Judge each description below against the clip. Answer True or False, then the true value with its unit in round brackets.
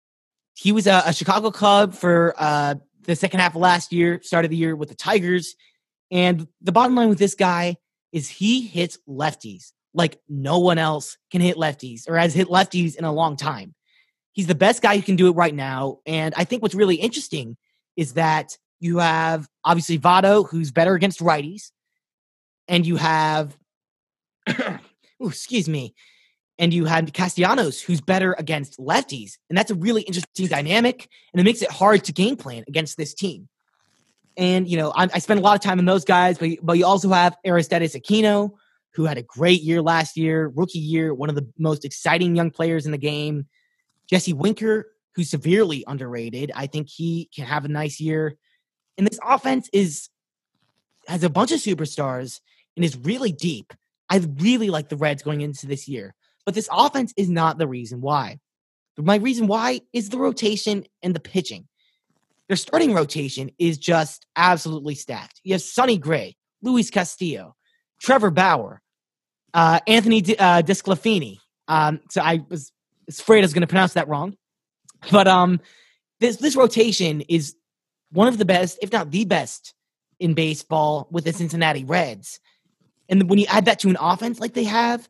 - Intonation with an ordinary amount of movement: True (4.2 semitones)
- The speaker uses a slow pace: False (180 wpm)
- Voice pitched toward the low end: False (175 Hz)